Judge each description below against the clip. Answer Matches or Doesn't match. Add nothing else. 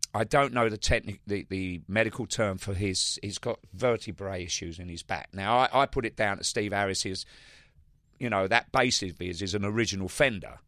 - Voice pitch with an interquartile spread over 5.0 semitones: Doesn't match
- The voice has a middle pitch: Doesn't match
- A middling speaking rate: Doesn't match